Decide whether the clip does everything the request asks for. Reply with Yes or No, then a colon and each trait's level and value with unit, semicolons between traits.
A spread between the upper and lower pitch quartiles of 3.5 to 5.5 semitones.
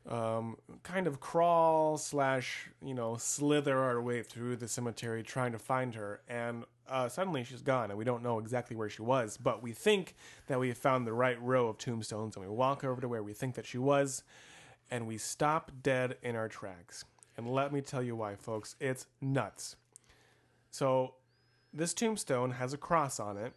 No: average, 2.9 semitones